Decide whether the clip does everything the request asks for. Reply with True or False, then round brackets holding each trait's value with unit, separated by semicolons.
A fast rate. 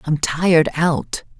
False (130 wpm)